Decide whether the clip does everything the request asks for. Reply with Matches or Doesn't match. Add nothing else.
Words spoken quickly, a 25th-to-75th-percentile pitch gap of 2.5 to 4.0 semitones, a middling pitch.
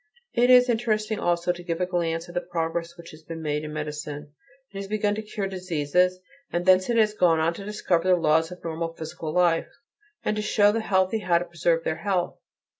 Matches